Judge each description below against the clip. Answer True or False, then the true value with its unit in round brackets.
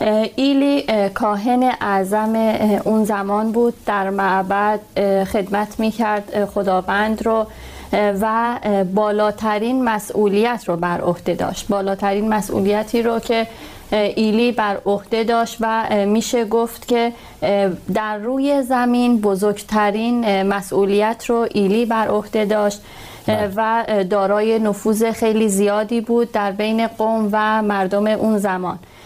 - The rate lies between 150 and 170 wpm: False (115 wpm)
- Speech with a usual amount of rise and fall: False (2.0 semitones)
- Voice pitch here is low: False (215 Hz)